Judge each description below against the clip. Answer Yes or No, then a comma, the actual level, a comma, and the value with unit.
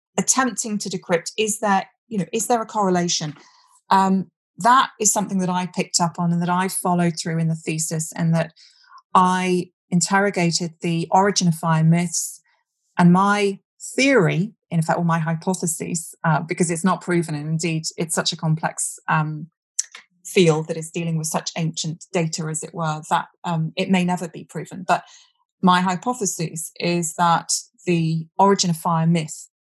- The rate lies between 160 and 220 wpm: Yes, average, 175 wpm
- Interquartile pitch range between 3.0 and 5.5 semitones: No, narrow, 2.6 semitones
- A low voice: No, medium, 175 Hz